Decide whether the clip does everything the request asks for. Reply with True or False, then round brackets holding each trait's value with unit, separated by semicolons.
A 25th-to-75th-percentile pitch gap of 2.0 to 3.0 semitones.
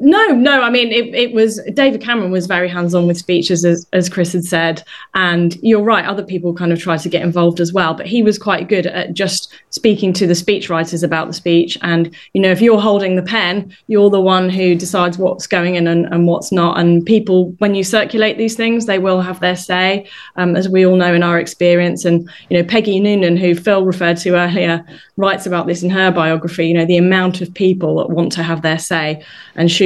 True (2.5 semitones)